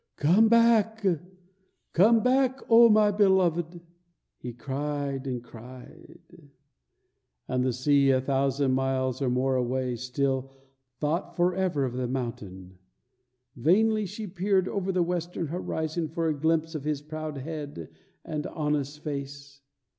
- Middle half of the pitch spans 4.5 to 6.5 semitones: Yes, average, 5.3 semitones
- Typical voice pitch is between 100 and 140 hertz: No, medium, 150 Hz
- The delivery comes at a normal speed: No, slow, 125 wpm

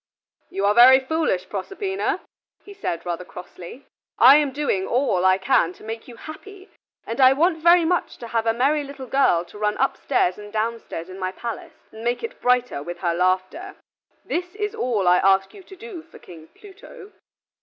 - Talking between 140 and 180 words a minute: No, average, 190 wpm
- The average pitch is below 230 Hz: No, high, 245 Hz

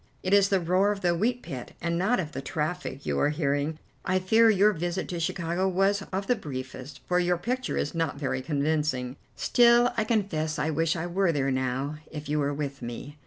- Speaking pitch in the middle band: Yes, medium, 170 Hz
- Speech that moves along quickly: Yes, fast, 215 wpm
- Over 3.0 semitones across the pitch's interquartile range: Yes, average, 4.9 semitones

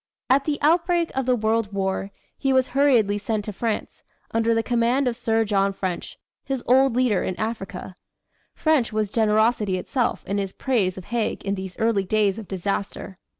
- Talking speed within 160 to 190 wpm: Yes, average, 180 wpm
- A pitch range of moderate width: Yes, average, 4.1 semitones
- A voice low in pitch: No, high, 225 Hz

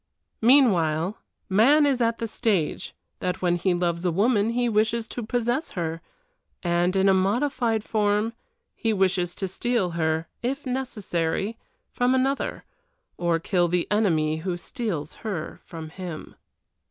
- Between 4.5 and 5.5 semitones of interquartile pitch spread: Yes, average, 5.1 semitones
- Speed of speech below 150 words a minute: Yes, average, 140 wpm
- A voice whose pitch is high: Yes, high, 195 Hz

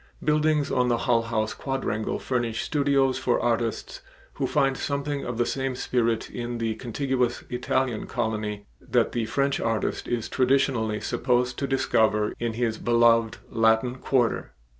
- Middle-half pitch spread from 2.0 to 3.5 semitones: Yes, average, 2.8 semitones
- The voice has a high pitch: No, low, 120 Hz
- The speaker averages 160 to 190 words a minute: No, average, 145 wpm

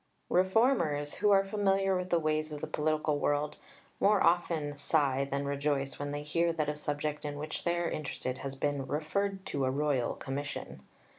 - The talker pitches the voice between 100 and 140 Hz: No, medium, 150 Hz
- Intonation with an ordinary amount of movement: Yes, average, 3.2 semitones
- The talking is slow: No, average, 180 wpm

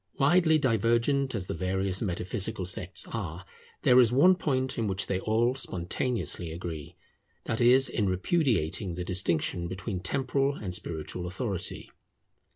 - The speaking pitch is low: Yes, low, 100 Hz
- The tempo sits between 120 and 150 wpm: Yes, average, 140 wpm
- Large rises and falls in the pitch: Yes, wide, 6.0 semitones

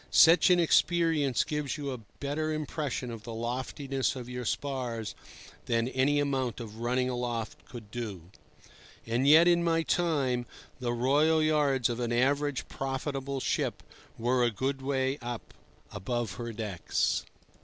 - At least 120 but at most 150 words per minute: Yes, average, 145 wpm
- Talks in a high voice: No, low, 130 Hz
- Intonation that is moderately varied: Yes, average, 3.4 semitones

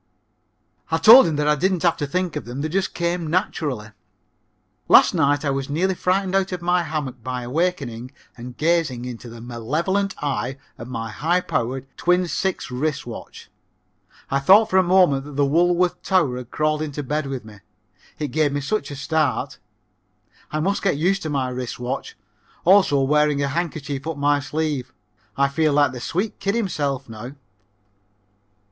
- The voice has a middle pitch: Yes, medium, 150 Hz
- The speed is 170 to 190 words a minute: Yes, average, 180 wpm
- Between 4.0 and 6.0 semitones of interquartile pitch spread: Yes, average, 4.8 semitones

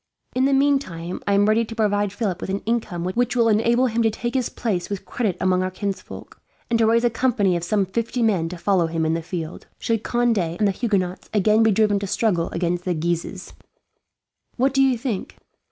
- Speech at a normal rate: No, fast, 220 wpm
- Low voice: No, high, 205 Hz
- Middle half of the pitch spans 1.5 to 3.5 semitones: No, average, 4.2 semitones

